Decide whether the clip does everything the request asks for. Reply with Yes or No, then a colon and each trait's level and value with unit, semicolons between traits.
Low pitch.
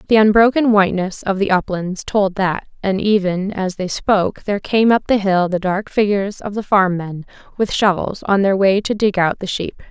No: high, 195 Hz